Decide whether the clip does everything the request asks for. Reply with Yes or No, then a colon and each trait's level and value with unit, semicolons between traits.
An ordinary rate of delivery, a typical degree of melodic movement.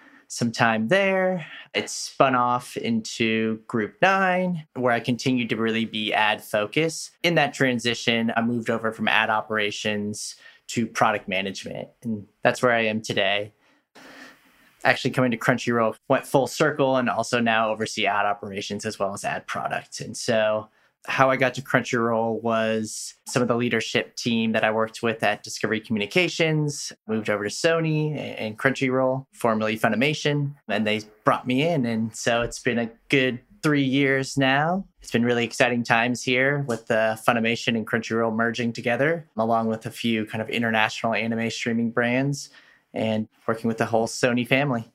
Yes: average, 165 wpm; average, 3.2 semitones